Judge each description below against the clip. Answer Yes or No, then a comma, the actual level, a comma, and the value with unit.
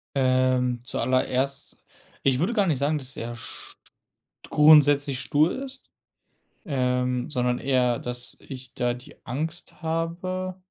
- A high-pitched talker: No, low, 135 Hz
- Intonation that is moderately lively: Yes, average, 3.9 semitones